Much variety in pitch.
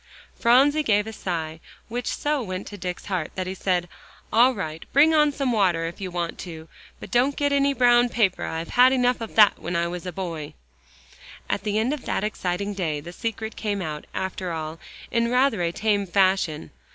Yes: wide, 5.8 semitones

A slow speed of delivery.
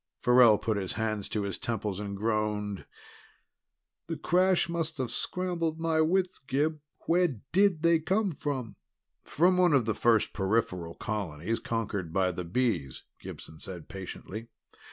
No: average, 145 wpm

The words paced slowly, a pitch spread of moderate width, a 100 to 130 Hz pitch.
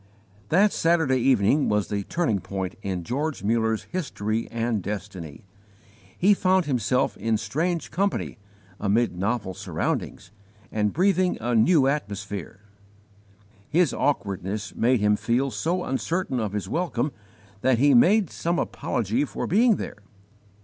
No: slow, 130 wpm; wide, 7.8 semitones; low, 120 Hz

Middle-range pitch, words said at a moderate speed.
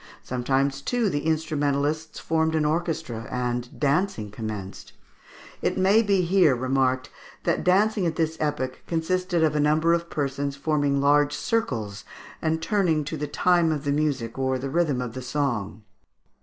Yes: medium, 150 Hz; average, 155 wpm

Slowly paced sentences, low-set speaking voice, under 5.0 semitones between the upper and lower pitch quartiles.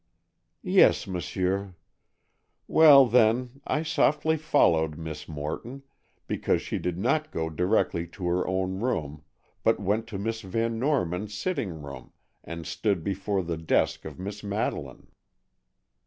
No: slow, 130 wpm; low, 100 Hz; wide, 5.6 semitones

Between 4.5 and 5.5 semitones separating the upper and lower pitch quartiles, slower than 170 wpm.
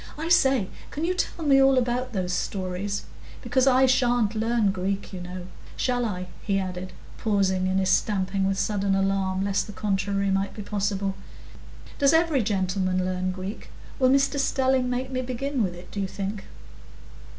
No: average, 5.0 semitones; average, 175 wpm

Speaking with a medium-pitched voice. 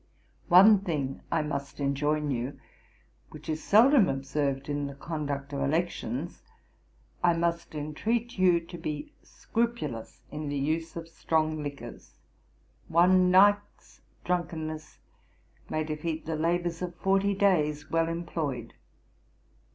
Yes: medium, 160 Hz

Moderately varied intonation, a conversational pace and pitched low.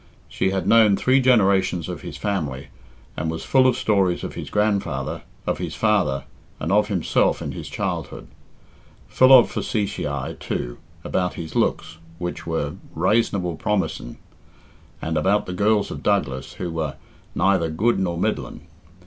Yes: average, 4.6 semitones; average, 150 wpm; very low, 95 Hz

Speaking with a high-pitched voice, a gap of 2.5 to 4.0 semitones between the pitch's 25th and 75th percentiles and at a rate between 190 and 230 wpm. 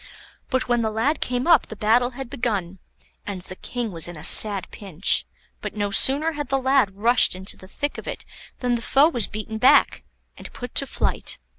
No: high, 235 Hz; average, 4.5 semitones; fast, 205 wpm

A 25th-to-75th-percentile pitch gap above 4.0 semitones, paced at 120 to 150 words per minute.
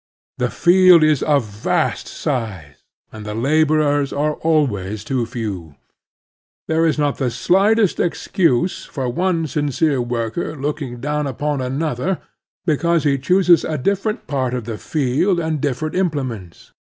Yes: average, 4.8 semitones; average, 140 wpm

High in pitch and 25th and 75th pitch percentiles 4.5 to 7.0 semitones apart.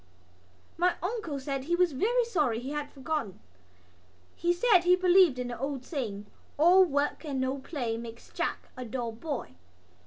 Yes: very high, 285 Hz; wide, 5.6 semitones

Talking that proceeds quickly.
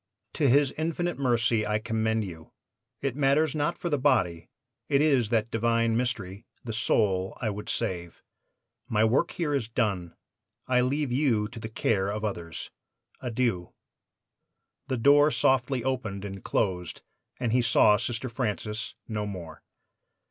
No: average, 150 wpm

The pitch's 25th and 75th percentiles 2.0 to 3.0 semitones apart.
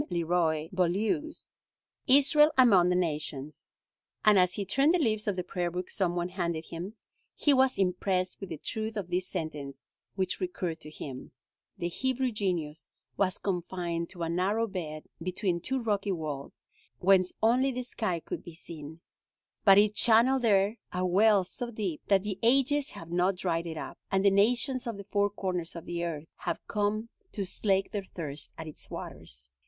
No: average, 4.1 semitones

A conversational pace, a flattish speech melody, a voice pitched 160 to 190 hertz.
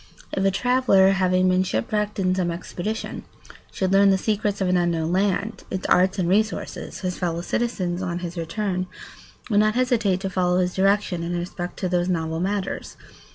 Yes: average, 180 wpm; narrow, 2.2 semitones; medium, 185 Hz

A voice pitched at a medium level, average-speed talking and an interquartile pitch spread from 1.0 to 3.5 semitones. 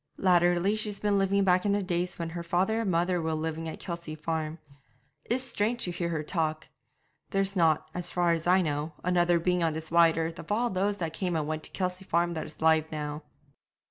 No: medium, 175 Hz; fast, 220 wpm; average, 2.8 semitones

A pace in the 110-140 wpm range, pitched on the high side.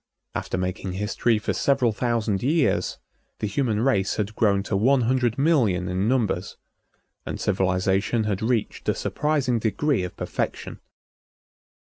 No: slow, 135 wpm; low, 110 Hz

